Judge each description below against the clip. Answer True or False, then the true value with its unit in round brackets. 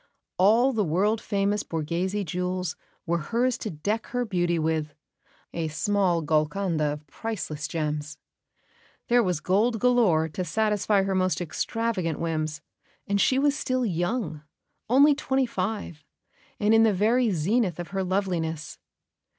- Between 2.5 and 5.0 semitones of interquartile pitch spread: False (5.5 semitones)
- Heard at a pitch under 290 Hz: True (185 Hz)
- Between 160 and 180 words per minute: False (140 wpm)